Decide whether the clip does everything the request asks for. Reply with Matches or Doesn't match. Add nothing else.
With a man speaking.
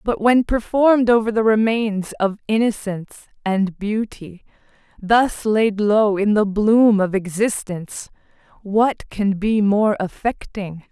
Doesn't match